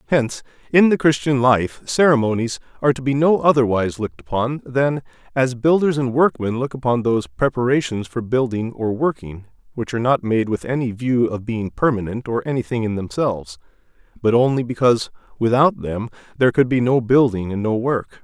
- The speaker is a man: Yes, male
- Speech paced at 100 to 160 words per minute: No, average, 175 wpm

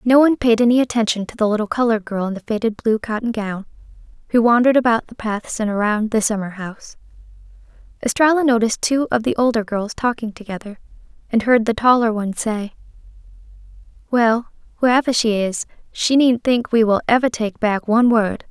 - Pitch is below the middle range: No, high, 225 Hz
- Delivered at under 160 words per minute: No, average, 180 wpm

